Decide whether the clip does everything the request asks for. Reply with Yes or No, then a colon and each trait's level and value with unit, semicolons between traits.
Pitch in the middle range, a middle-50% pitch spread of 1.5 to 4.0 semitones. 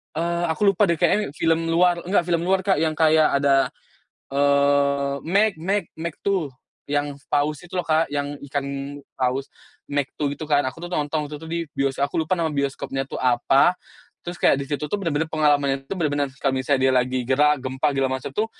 Yes: medium, 145 Hz; average, 3.3 semitones